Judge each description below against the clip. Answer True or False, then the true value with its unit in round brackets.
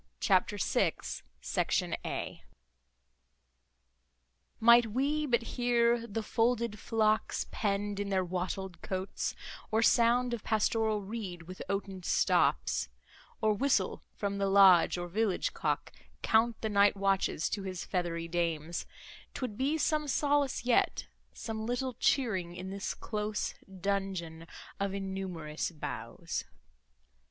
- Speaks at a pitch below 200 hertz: False (205 Hz)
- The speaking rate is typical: False (115 wpm)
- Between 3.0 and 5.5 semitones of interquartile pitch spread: True (3.9 semitones)